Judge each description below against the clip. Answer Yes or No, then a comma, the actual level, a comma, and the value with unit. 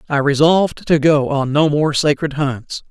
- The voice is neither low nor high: Yes, medium, 150 Hz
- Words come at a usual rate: Yes, average, 185 wpm